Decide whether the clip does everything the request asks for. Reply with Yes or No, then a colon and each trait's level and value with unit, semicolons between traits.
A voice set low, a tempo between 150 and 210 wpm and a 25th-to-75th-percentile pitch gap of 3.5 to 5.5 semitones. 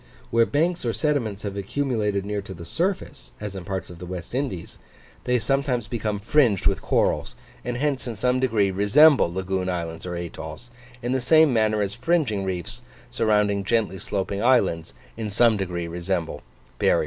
Yes: low, 105 Hz; average, 175 wpm; average, 4.8 semitones